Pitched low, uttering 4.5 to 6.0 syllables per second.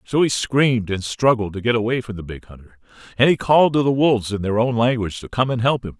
No: low, 115 Hz; 6.4 syllables/s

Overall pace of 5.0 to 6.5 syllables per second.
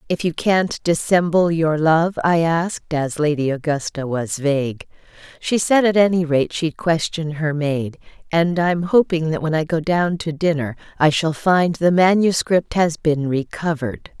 No: 4.4 syllables/s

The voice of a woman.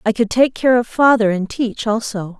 Yes: female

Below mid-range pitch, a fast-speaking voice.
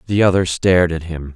Yes: very low, 85 Hz; fast, 220 wpm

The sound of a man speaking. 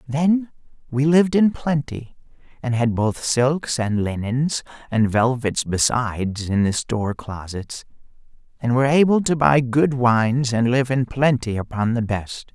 Yes: male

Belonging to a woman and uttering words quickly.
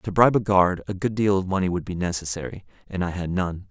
No: male; fast, 260 wpm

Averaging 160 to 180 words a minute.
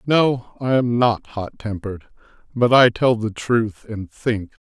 Yes: average, 165 wpm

